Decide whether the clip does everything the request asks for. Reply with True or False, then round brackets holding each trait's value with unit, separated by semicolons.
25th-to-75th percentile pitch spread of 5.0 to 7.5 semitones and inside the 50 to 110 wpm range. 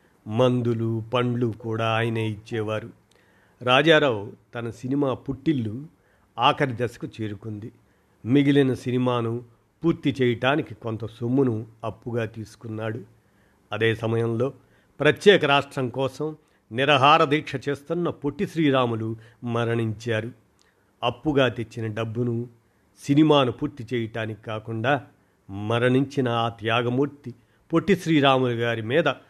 False (3.6 semitones; 90 wpm)